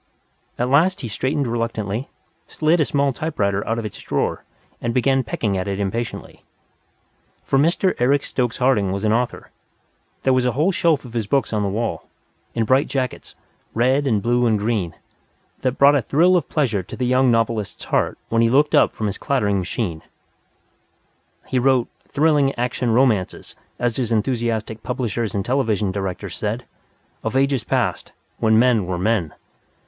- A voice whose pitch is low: Yes, low, 120 Hz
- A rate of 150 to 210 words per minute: Yes, average, 170 wpm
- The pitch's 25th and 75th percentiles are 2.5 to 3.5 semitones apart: No, average, 3.9 semitones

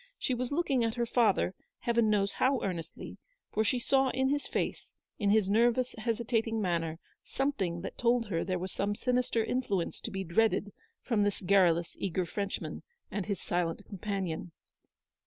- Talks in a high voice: Yes, high, 210 Hz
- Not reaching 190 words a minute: Yes, average, 165 wpm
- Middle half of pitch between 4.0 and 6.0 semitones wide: Yes, average, 4.3 semitones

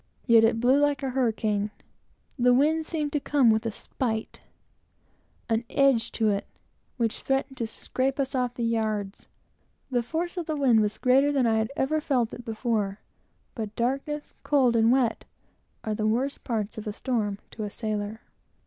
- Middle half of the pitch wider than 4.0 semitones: No, average, 3.6 semitones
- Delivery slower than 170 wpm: No, average, 180 wpm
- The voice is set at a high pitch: Yes, high, 240 Hz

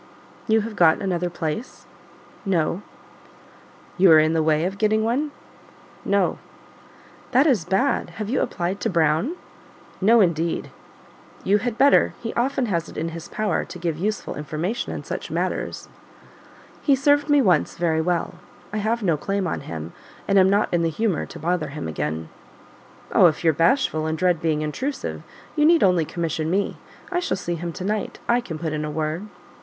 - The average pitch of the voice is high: No, medium, 180 Hz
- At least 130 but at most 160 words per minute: No, average, 180 wpm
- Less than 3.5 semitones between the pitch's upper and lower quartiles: No, wide, 5.4 semitones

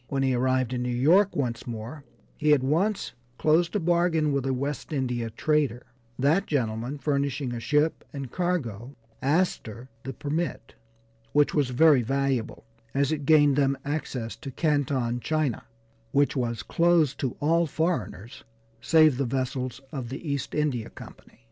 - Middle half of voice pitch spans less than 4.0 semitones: Yes, average, 3.6 semitones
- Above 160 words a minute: No, average, 155 wpm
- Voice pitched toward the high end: No, medium, 140 Hz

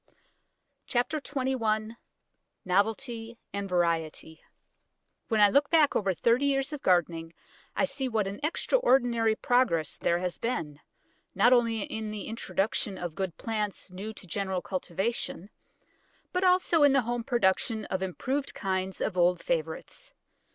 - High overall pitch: Yes, high, 220 Hz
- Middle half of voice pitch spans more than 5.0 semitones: Yes, wide, 5.5 semitones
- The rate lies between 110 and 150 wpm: Yes, slow, 135 wpm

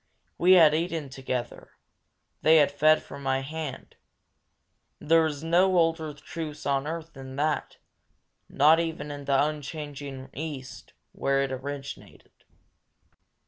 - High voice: No, medium, 150 Hz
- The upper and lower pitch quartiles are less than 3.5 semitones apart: Yes, average, 2.8 semitones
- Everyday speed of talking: No, slow, 130 wpm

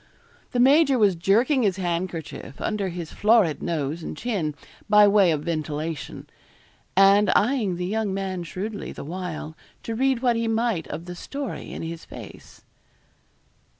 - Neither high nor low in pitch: No, high, 195 Hz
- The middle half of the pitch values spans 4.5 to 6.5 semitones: Yes, average, 5.0 semitones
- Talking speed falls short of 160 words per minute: Yes, average, 150 wpm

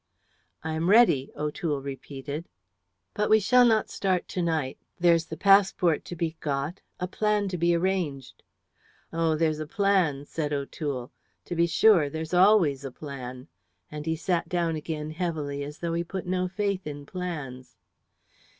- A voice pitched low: No, medium, 165 Hz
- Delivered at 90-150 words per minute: No, average, 160 wpm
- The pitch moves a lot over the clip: No, average, 3.9 semitones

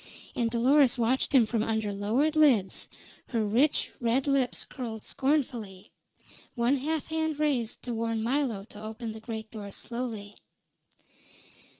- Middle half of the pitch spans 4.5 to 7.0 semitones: No, average, 3.8 semitones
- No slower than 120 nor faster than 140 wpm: Yes, slow, 135 wpm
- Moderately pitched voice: No, high, 235 Hz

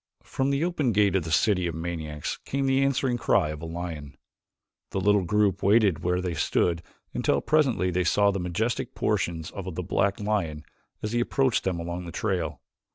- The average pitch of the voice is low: Yes, very low, 95 Hz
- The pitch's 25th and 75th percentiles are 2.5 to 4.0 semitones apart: No, average, 4.5 semitones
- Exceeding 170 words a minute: Yes, average, 190 wpm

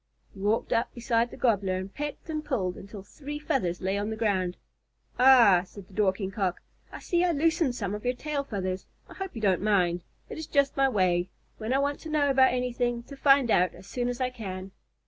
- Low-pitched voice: No, high, 230 Hz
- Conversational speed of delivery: No, fast, 225 wpm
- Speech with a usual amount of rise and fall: No, wide, 6.1 semitones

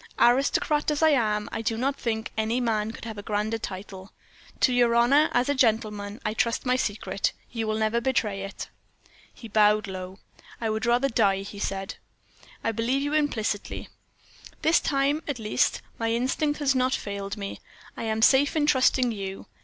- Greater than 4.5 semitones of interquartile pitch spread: No, average, 3.6 semitones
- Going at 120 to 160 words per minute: No, average, 180 wpm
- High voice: Yes, high, 225 Hz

